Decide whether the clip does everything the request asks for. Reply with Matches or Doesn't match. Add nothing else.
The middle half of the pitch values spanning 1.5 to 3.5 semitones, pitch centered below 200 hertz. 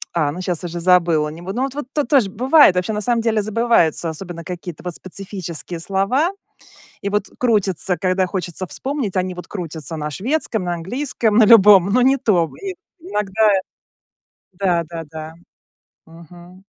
Doesn't match